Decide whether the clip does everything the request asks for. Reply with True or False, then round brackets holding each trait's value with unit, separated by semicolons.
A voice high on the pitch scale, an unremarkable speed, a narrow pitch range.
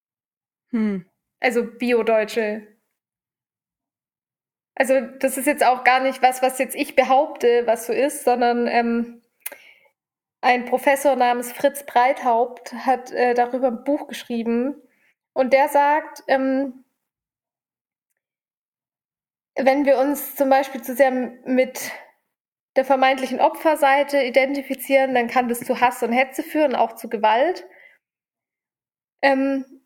False (260 Hz; 115 wpm; 2.1 semitones)